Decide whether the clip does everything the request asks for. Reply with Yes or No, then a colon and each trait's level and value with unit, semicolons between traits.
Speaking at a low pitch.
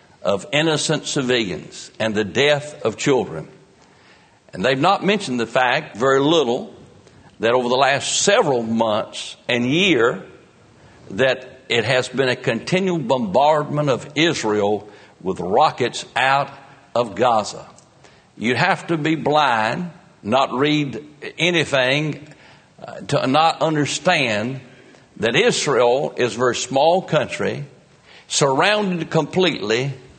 No: medium, 145 Hz